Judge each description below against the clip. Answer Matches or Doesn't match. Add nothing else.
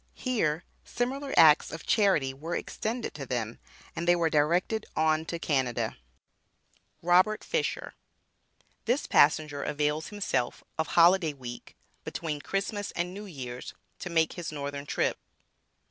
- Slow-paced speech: Matches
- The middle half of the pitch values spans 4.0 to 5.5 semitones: Matches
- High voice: Doesn't match